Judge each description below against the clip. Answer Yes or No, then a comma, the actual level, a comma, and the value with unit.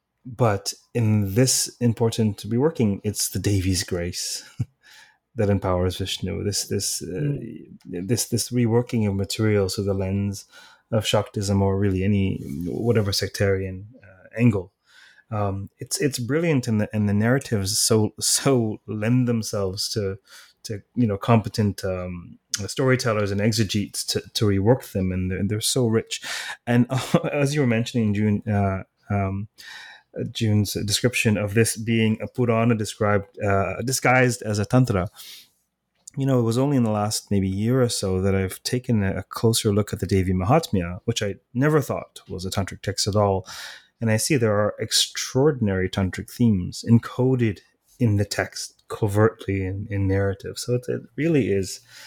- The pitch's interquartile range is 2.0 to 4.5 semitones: Yes, average, 3.4 semitones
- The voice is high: No, low, 105 Hz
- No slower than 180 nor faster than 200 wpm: No, average, 155 wpm